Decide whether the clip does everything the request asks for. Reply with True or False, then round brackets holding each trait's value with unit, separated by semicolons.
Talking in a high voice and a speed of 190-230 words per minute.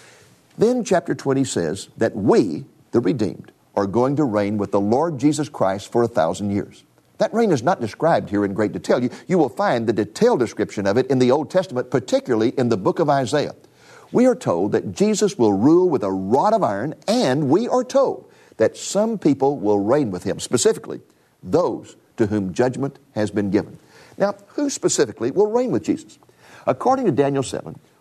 False (135 Hz; 195 wpm)